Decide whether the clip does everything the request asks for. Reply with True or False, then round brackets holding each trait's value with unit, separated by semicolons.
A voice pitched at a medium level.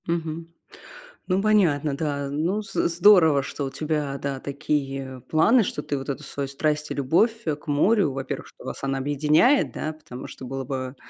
True (150 Hz)